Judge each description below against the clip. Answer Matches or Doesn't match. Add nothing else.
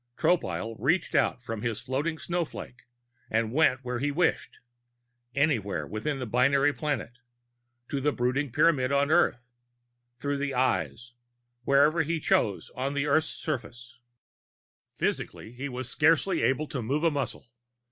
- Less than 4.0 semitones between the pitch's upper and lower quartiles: Matches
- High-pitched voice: Doesn't match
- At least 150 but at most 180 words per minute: Doesn't match